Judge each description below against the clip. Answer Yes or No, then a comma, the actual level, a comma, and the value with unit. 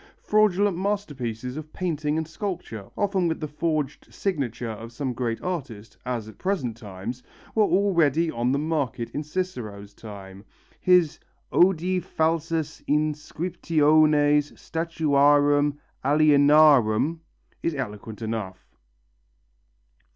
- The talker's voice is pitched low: No, medium, 150 Hz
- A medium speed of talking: No, slow, 105 wpm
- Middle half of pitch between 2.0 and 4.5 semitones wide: No, wide, 5.6 semitones